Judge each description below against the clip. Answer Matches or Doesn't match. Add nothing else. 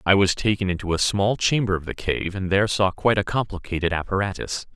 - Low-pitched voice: Matches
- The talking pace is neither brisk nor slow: Doesn't match